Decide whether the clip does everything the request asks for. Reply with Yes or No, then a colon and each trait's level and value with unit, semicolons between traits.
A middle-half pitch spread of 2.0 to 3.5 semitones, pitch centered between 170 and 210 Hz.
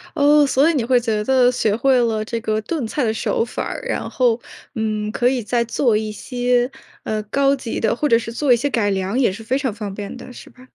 No: average, 3.1 semitones; high, 235 Hz